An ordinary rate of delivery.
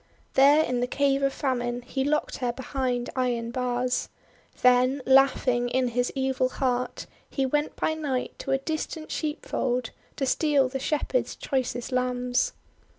Yes: average, 155 wpm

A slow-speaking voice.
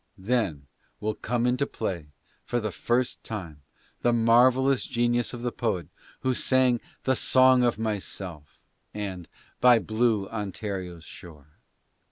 Yes: slow, 130 wpm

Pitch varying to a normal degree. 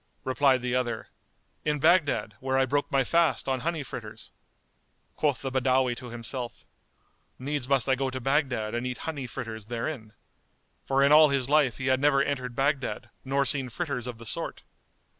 No: narrow, 2.3 semitones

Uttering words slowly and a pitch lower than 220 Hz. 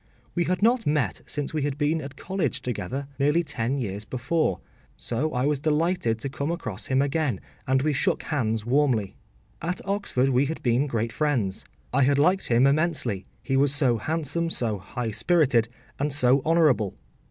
No: average, 175 wpm; medium, 140 Hz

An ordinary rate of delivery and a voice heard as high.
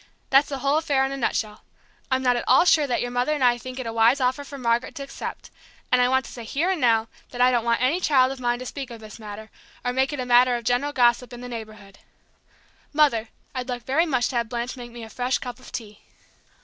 No: fast, 265 wpm; very high, 250 Hz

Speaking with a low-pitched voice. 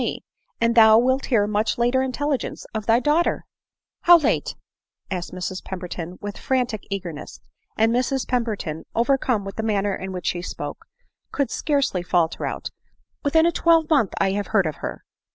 No: high, 220 Hz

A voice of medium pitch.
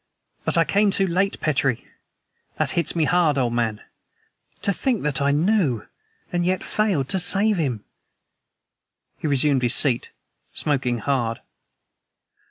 Yes: medium, 150 Hz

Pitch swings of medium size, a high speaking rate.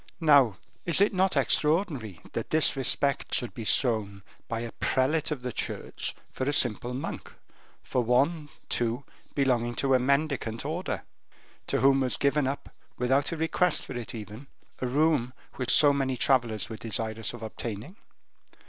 No: average, 3.8 semitones; average, 160 wpm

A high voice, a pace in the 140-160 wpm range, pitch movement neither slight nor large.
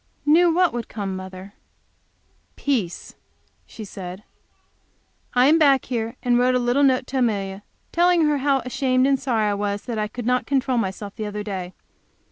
No: high, 245 Hz; average, 175 wpm; average, 4.9 semitones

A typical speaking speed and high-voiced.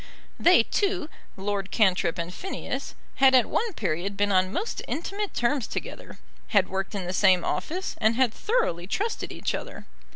Yes: average, 165 wpm; high, 210 Hz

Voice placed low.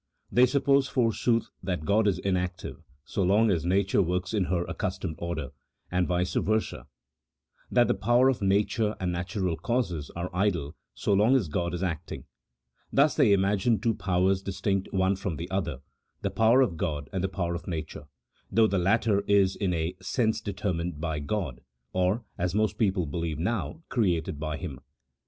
Yes: very low, 95 Hz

